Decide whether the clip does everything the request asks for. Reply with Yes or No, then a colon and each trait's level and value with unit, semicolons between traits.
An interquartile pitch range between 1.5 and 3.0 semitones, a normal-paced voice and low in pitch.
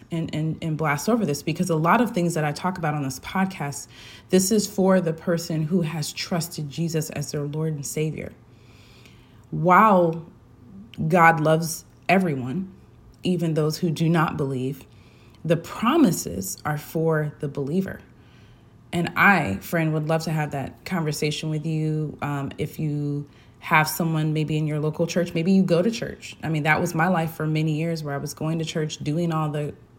No: narrow, 2.6 semitones; average, 185 wpm; medium, 155 Hz